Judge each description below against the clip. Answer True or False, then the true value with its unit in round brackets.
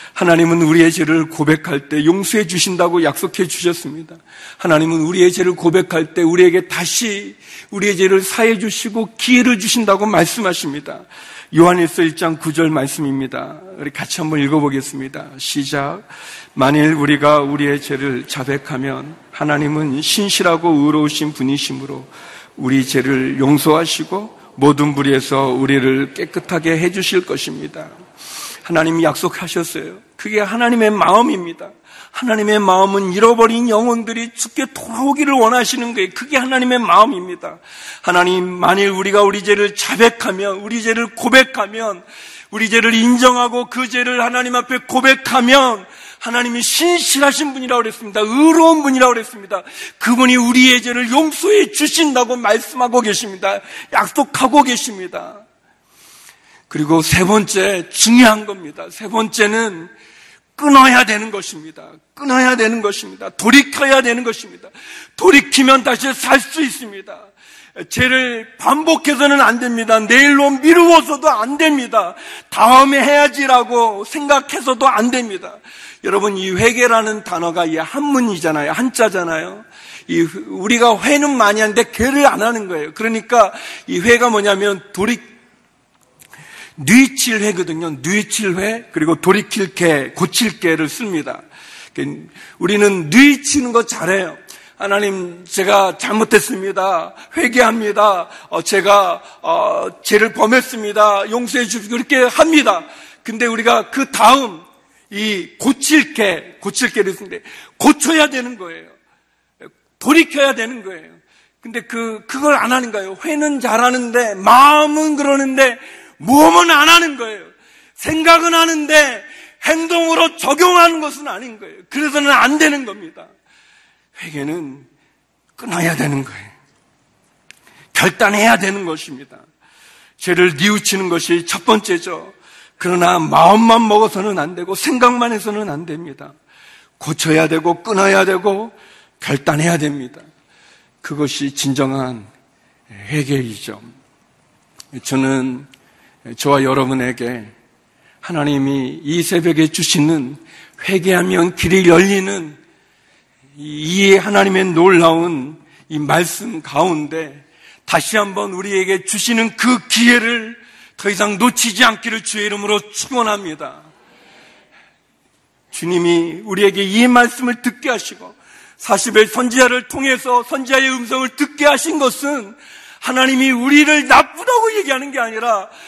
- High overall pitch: True (210 Hz)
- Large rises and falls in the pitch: True (7.0 semitones)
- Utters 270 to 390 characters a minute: True (295 characters per minute)